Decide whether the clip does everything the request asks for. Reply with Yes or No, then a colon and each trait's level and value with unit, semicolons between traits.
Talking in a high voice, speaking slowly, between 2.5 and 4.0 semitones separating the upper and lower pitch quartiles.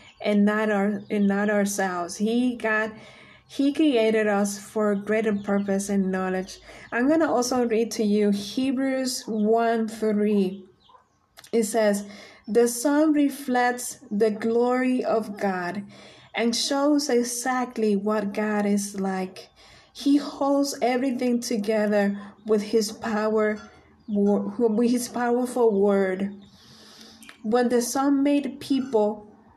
Yes: high, 220 Hz; slow, 120 wpm; average, 3.1 semitones